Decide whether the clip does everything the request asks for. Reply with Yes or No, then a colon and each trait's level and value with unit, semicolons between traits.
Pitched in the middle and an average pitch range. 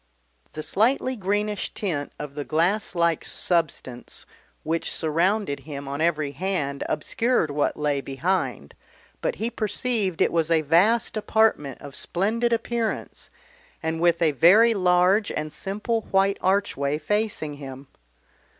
No: medium, 170 Hz; wide, 5.9 semitones